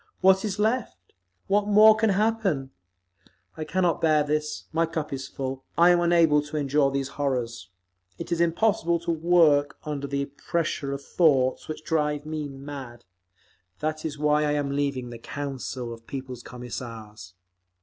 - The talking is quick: No, average, 160 wpm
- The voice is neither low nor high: Yes, medium, 150 Hz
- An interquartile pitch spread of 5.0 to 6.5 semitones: No, average, 3.7 semitones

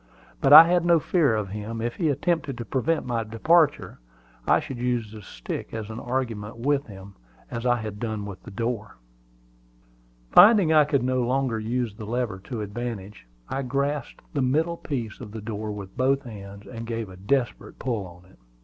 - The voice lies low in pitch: Yes, low, 120 Hz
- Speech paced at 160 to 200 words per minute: Yes, average, 190 wpm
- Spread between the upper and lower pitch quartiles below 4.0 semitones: No, average, 4.3 semitones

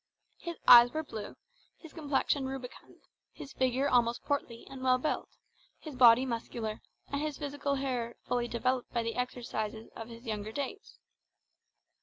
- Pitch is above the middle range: Yes, very high, 250 Hz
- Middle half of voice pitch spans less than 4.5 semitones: Yes, average, 3.2 semitones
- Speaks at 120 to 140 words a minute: No, average, 150 wpm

